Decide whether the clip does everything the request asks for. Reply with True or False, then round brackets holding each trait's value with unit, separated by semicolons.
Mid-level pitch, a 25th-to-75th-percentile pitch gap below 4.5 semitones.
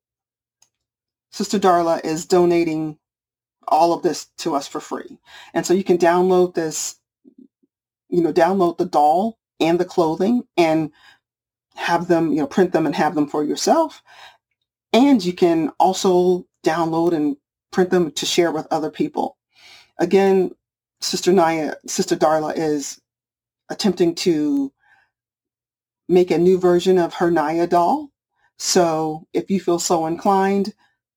True (175 Hz; 3.6 semitones)